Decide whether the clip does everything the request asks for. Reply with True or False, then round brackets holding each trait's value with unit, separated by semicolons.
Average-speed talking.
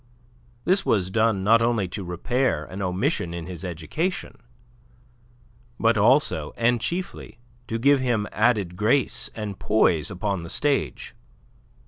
False (130 wpm)